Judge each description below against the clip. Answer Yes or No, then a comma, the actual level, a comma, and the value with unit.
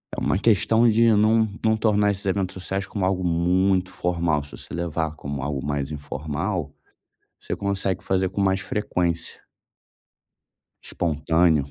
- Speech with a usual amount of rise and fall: Yes, average, 3.9 semitones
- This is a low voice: Yes, very low, 90 Hz